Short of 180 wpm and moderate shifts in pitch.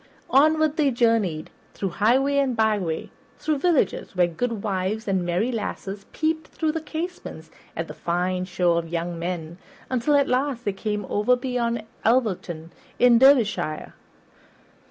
No: average, 140 wpm; wide, 6.6 semitones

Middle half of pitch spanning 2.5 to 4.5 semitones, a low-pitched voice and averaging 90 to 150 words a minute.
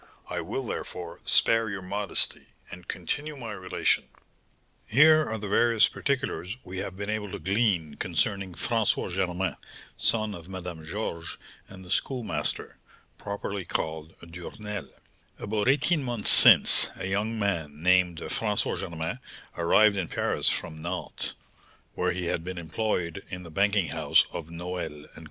Yes: average, 3.7 semitones; very low, 95 Hz; average, 145 wpm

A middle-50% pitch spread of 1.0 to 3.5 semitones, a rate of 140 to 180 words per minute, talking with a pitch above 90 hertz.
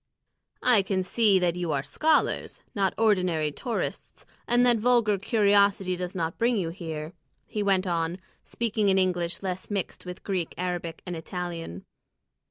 Yes: average, 3.2 semitones; average, 155 wpm; medium, 185 Hz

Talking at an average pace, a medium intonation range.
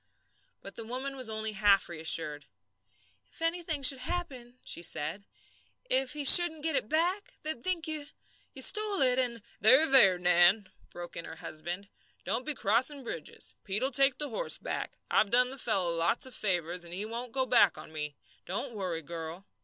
No: average, 185 wpm; wide, 7.5 semitones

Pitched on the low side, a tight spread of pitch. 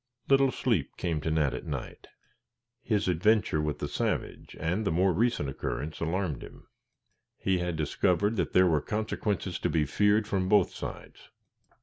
No: very low, 90 Hz; average, 4.8 semitones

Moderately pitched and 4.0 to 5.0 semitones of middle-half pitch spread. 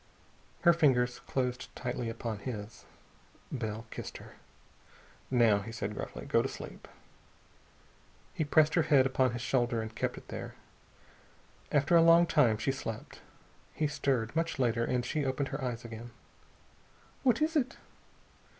No: low, 125 Hz; average, 4.4 semitones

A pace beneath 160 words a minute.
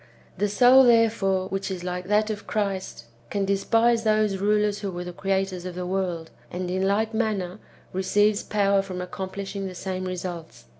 No: average, 170 wpm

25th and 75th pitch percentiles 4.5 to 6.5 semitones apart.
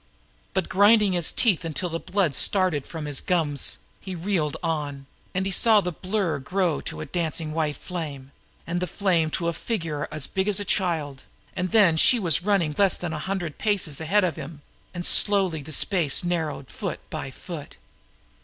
No: average, 3.8 semitones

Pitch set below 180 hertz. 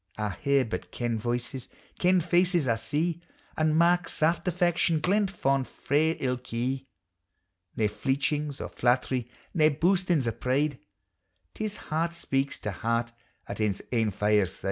Yes: medium, 140 Hz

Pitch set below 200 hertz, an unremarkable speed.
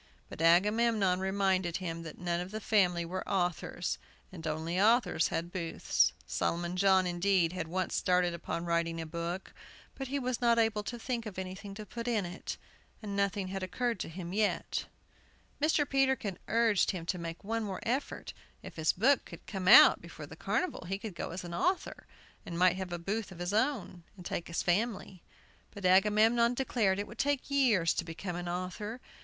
Yes: high, 190 Hz; average, 190 wpm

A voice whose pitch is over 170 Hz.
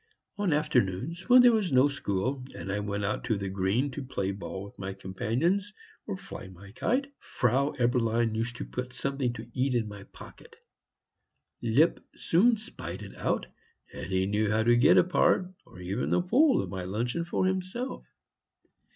No: low, 120 Hz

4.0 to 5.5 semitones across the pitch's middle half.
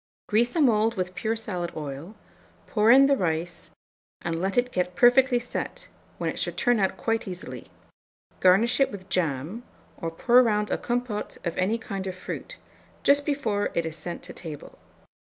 Yes: average, 5.2 semitones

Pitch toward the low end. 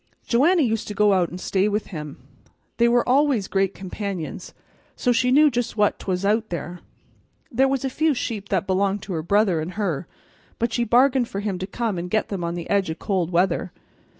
No: high, 200 Hz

